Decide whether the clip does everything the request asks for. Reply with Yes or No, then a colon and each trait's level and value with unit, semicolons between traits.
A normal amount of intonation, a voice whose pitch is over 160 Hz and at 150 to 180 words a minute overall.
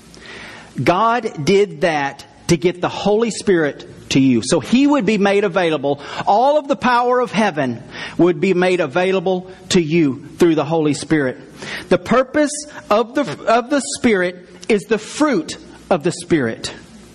No: wide, 6.1 semitones; medium, 185 Hz; average, 160 wpm